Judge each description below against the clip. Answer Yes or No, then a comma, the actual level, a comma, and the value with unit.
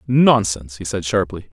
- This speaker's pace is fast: No, average, 150 wpm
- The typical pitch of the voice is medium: No, low, 100 Hz